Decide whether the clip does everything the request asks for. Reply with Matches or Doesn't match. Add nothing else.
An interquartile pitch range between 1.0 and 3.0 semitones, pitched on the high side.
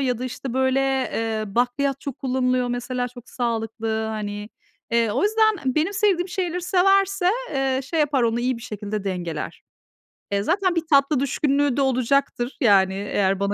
Doesn't match